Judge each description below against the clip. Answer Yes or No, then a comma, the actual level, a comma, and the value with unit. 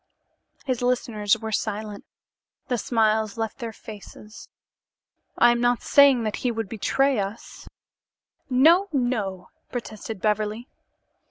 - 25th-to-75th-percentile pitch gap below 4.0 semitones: Yes, narrow, 2.6 semitones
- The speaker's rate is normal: No, slow, 120 wpm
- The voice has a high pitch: Yes, high, 225 Hz